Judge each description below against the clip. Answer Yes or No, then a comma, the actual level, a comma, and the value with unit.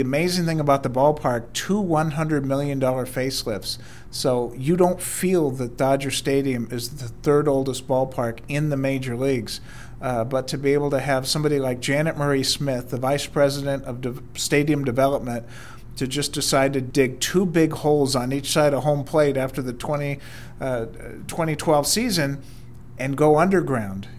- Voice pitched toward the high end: No, low, 135 Hz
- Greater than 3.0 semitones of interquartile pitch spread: No, narrow, 2.5 semitones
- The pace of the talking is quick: No, average, 165 wpm